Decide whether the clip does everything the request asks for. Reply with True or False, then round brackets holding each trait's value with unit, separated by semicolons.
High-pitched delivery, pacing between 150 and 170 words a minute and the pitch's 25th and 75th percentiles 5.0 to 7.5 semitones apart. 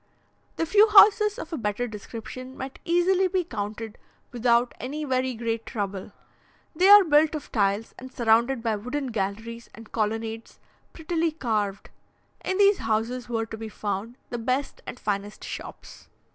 True (240 Hz; 155 wpm; 5.6 semitones)